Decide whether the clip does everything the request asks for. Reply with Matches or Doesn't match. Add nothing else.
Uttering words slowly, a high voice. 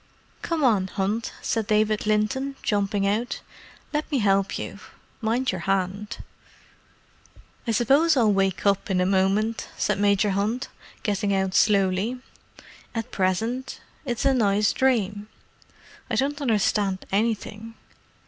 Matches